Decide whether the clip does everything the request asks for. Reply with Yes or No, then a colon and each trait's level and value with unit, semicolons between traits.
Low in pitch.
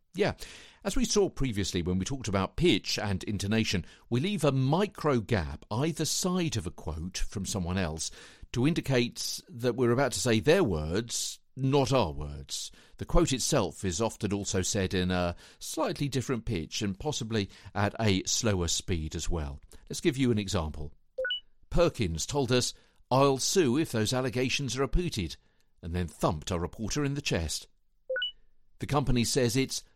Yes: low, 110 Hz